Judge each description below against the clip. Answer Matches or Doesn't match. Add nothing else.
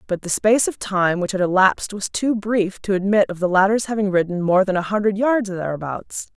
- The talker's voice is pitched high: Matches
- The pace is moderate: Doesn't match